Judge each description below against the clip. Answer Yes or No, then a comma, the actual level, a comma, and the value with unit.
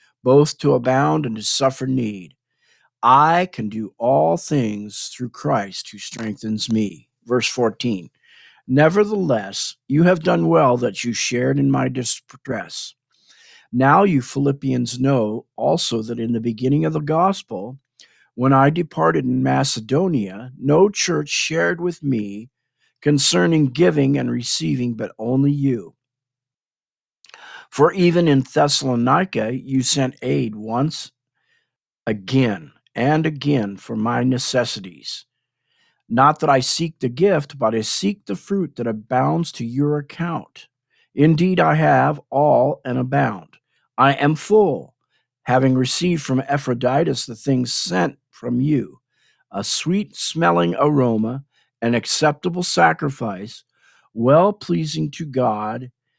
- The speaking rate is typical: No, slow, 125 wpm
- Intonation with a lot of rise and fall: No, average, 4.2 semitones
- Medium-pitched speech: No, low, 130 Hz